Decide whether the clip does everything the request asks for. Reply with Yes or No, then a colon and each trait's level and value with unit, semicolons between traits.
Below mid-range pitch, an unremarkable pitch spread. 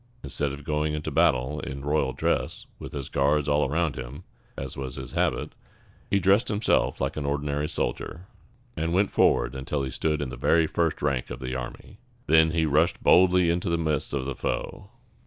Yes: very low, 75 Hz; average, 3.2 semitones